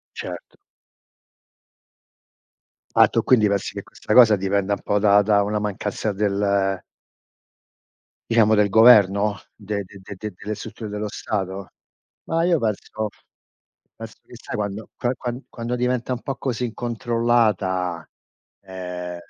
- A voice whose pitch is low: Yes, low, 105 Hz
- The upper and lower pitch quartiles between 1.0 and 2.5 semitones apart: No, average, 2.9 semitones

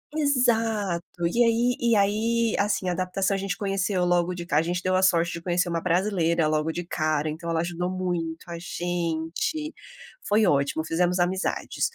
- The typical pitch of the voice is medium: Yes, medium, 180 Hz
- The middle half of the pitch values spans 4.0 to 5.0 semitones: No, average, 3.1 semitones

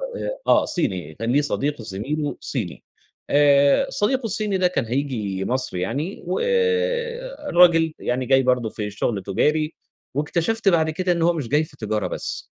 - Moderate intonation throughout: No, wide, 7.4 semitones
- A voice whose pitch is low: No, medium, 150 Hz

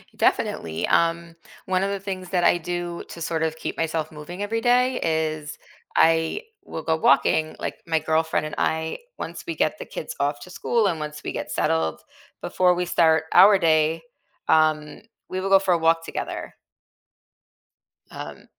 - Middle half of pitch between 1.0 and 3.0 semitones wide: Yes, average, 2.7 semitones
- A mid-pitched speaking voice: Yes, medium, 165 Hz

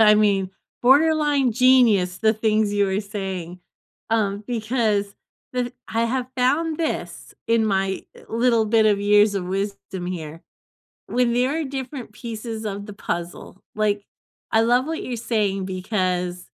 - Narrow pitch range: No, average, 3.8 semitones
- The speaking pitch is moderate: No, high, 215 Hz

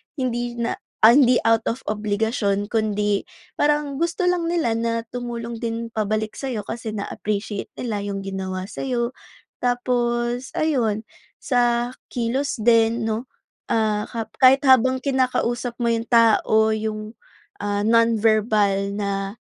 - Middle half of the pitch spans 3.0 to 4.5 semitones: No, narrow, 2.4 semitones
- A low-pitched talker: No, high, 230 Hz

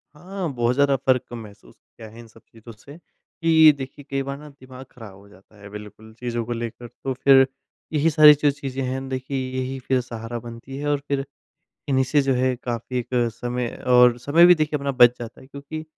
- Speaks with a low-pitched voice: Yes, low, 130 Hz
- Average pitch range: Yes, average, 3.1 semitones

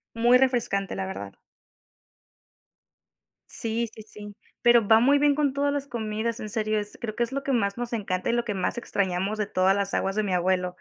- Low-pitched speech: No, high, 215 Hz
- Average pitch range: Yes, average, 3.3 semitones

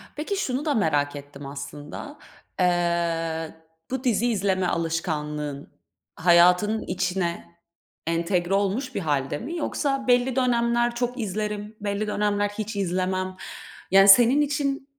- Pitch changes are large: Yes, wide, 6.1 semitones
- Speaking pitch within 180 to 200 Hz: Yes, high, 195 Hz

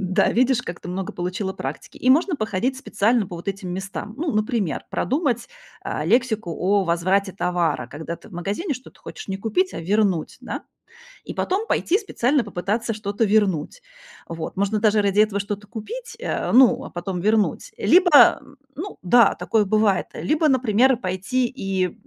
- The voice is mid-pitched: No, high, 210 Hz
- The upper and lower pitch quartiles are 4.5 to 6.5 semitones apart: Yes, average, 5.2 semitones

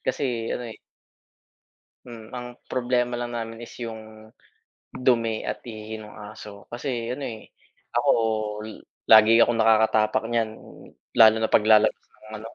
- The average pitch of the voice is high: No, low, 115 Hz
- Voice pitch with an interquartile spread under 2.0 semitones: Yes, narrow, 1.6 semitones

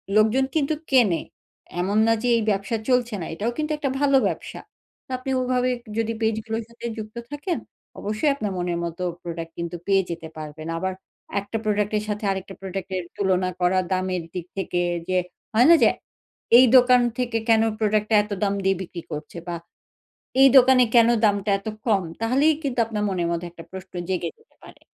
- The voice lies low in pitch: No, high, 210 Hz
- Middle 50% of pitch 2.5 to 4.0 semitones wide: No, average, 4.7 semitones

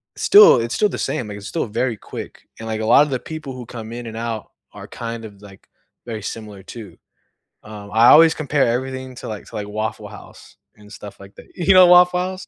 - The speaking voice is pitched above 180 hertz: No, low, 115 Hz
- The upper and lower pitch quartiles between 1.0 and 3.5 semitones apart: No, average, 4.4 semitones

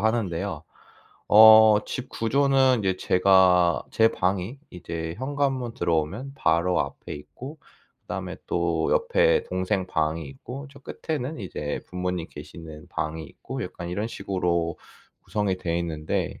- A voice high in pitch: No, very low, 95 Hz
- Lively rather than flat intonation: Yes, wide, 6.7 semitones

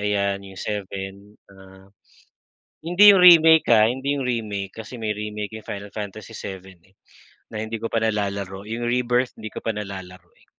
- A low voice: Yes, low, 105 Hz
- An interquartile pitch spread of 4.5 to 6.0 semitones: No, average, 3.1 semitones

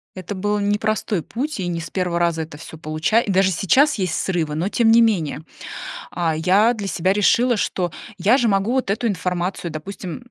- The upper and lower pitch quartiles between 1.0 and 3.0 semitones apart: No, average, 4.0 semitones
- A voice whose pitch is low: No, high, 190 Hz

